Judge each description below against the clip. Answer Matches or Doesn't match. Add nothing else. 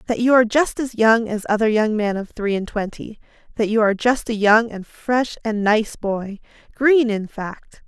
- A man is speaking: Doesn't match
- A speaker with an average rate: Doesn't match